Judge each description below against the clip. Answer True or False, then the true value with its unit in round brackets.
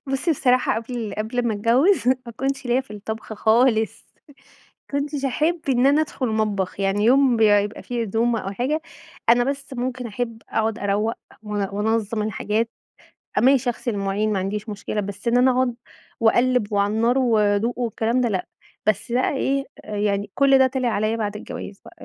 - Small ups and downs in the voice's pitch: False (3.4 semitones)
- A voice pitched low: False (230 Hz)